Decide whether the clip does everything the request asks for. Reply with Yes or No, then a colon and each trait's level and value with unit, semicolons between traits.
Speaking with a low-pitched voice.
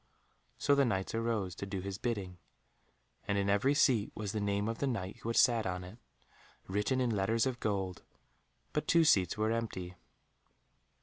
Yes: low, 105 Hz